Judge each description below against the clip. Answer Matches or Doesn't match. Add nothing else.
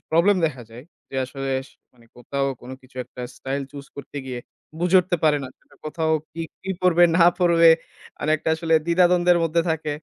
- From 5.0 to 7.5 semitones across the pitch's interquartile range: Doesn't match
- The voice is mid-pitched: Matches